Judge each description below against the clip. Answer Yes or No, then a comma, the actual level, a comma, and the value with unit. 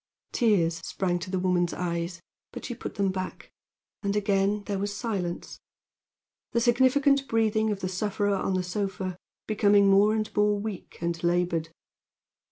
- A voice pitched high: Yes, high, 200 Hz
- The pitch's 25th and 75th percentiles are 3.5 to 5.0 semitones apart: No, average, 2.9 semitones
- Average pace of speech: Yes, average, 155 wpm